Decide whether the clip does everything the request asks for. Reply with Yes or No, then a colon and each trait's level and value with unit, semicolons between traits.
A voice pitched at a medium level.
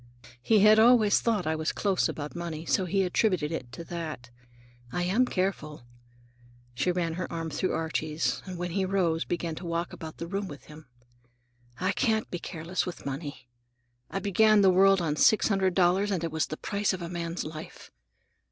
Yes: medium, 175 Hz